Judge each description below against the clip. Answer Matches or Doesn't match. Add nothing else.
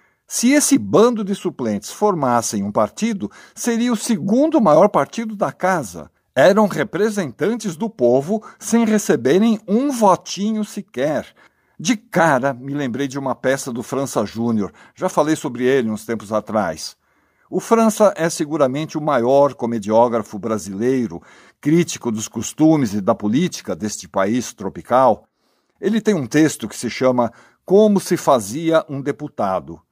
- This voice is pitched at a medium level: Matches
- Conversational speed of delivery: Matches